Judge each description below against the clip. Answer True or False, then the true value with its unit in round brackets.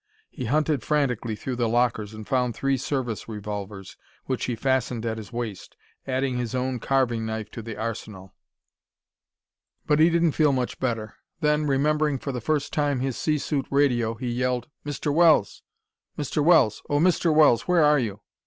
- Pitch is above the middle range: False (125 Hz)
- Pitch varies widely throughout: False (4.3 semitones)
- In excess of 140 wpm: True (170 wpm)